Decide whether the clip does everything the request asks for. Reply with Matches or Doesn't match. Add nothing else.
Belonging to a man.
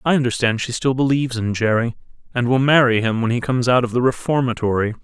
Matches